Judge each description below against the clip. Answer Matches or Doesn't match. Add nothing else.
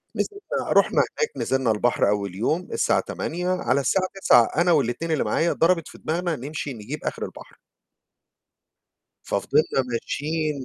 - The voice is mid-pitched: Matches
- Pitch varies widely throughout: Matches